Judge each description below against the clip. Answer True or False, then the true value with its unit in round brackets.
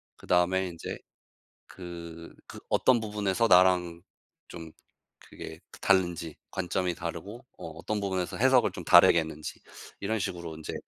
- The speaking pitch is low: True (90 Hz)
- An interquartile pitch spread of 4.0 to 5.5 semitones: False (2.7 semitones)